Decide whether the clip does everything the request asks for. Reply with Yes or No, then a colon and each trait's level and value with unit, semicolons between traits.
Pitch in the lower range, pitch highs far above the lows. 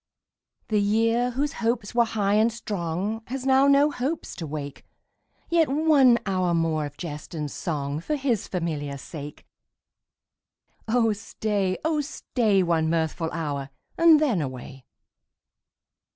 No: high, 205 Hz; wide, 7.6 semitones